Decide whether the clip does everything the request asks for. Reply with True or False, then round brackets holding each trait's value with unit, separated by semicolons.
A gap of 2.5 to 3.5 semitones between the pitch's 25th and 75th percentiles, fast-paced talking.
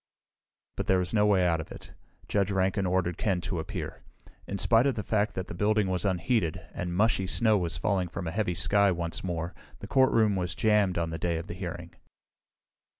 True (3.1 semitones; 210 wpm)